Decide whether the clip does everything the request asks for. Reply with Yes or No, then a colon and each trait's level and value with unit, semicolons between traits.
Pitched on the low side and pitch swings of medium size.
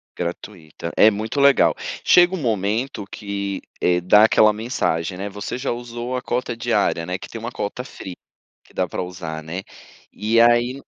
Yes: low, 105 Hz; average, 4.6 semitones